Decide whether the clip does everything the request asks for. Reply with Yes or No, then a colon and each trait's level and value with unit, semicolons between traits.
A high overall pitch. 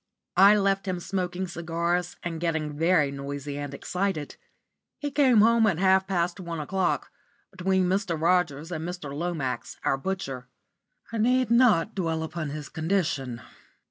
No: medium, 175 Hz